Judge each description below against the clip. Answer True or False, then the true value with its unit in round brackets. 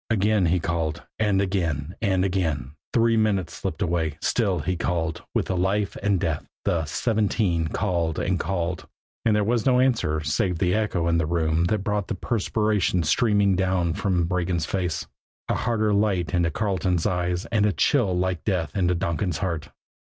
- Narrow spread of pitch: False (3.6 semitones)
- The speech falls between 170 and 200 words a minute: True (175 wpm)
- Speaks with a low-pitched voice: True (90 Hz)